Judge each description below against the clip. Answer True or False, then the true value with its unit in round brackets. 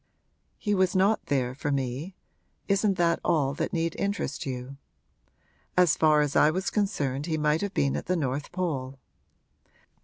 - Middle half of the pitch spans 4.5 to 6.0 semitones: True (5.2 semitones)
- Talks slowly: False (160 wpm)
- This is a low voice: False (155 Hz)